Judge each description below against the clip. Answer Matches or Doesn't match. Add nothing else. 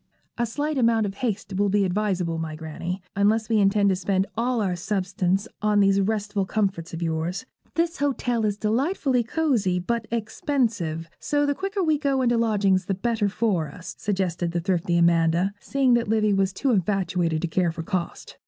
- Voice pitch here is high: Matches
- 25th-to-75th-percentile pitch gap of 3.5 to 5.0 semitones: Matches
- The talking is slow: Doesn't match